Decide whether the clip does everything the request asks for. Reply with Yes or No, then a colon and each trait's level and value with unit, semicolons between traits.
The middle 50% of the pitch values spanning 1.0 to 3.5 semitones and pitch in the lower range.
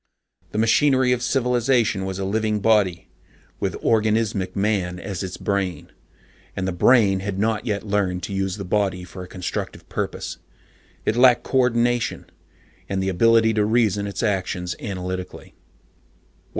Yes: average, 3.2 semitones; low, 100 Hz